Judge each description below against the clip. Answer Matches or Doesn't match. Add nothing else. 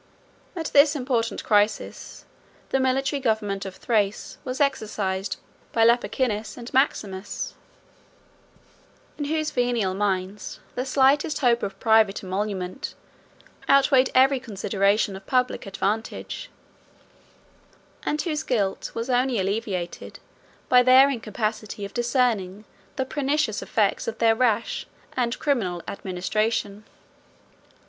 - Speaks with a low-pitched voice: Doesn't match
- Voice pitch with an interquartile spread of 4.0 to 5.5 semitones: Matches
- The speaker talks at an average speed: Doesn't match